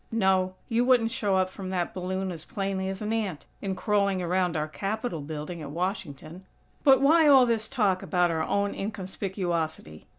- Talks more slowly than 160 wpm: No, average, 175 wpm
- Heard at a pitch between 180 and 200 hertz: Yes, high, 190 Hz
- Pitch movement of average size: Yes, average, 3.3 semitones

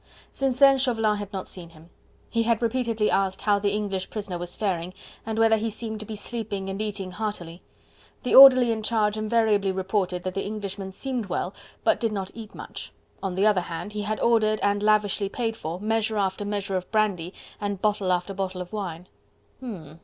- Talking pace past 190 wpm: Yes, average, 200 wpm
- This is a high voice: Yes, high, 205 Hz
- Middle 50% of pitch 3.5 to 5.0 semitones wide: No, narrow, 2.6 semitones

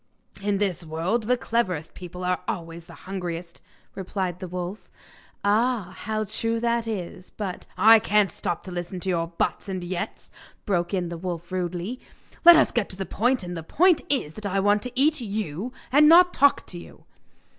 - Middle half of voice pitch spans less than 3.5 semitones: No, average, 4.4 semitones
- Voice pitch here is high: Yes, high, 195 Hz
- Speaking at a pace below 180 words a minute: No, average, 190 wpm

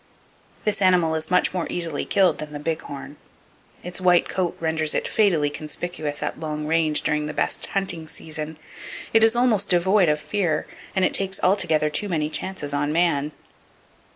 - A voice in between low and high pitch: Yes, medium, 165 Hz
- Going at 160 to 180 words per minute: Yes, average, 175 wpm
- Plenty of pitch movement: No, average, 3.5 semitones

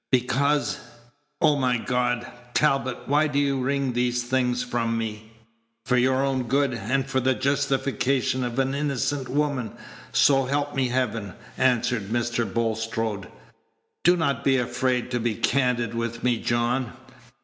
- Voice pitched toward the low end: Yes, low, 125 Hz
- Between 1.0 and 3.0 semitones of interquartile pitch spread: Yes, narrow, 2.4 semitones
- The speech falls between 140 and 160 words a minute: Yes, average, 145 wpm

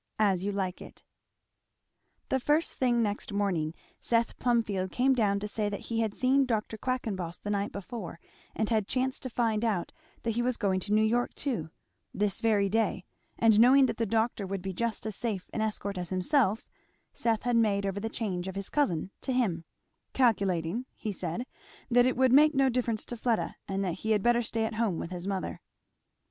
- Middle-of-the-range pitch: No, high, 220 Hz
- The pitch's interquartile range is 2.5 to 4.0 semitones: Yes, average, 3.5 semitones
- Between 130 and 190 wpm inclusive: No, average, 200 wpm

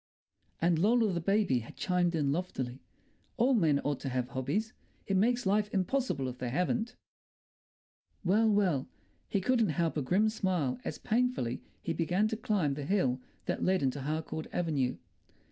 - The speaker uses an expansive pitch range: Yes, wide, 7.0 semitones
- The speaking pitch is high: No, medium, 175 Hz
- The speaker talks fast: No, average, 160 wpm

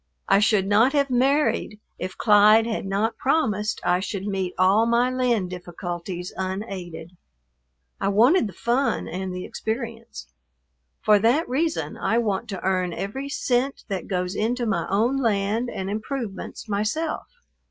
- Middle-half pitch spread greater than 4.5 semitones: No, average, 4.2 semitones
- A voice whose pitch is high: Yes, high, 210 Hz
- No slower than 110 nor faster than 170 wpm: Yes, average, 145 wpm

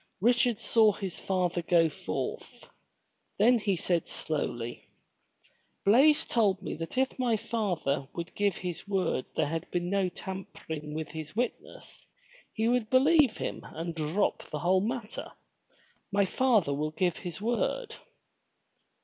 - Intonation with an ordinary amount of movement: No, wide, 5.9 semitones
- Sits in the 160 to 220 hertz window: Yes, high, 190 Hz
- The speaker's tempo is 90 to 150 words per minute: Yes, average, 140 wpm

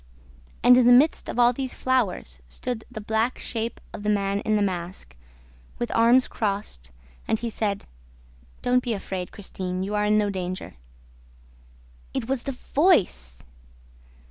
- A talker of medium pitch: No, high, 215 Hz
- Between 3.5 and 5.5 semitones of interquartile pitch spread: Yes, average, 4.2 semitones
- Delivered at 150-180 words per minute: Yes, average, 155 wpm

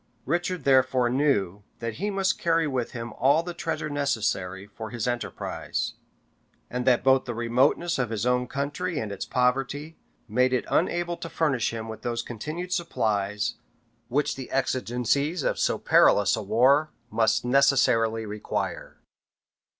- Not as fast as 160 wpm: Yes, average, 150 wpm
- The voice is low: Yes, low, 125 Hz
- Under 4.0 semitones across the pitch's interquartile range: No, average, 4.5 semitones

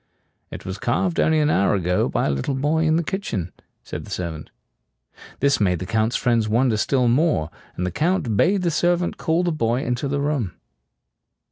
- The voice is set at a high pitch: No, low, 125 Hz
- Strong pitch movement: Yes, wide, 7.5 semitones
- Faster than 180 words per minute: Yes, average, 195 wpm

